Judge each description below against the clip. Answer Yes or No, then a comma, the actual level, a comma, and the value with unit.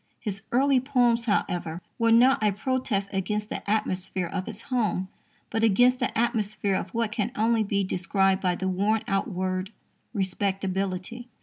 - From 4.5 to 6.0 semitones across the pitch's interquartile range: No, average, 3.5 semitones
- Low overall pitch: No, high, 205 Hz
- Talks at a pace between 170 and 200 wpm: No, average, 160 wpm